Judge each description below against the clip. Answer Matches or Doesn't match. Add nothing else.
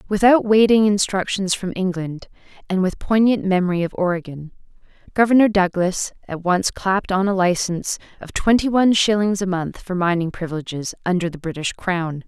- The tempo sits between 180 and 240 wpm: Doesn't match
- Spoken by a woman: Matches